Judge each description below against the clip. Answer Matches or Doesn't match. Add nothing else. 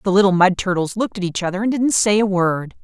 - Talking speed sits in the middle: Doesn't match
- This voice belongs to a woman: Matches